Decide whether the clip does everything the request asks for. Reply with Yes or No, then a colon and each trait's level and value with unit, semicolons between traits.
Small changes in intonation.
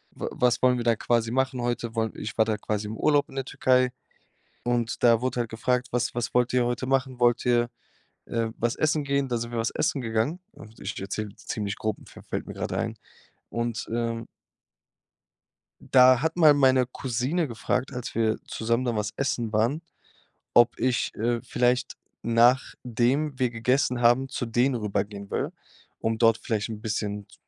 Yes: narrow, 2.2 semitones